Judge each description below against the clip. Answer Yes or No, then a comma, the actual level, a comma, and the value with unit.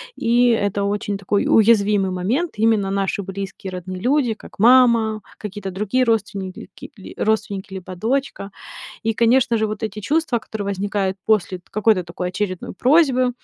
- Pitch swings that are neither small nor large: Yes, average, 3.0 semitones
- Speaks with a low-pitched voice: No, high, 210 Hz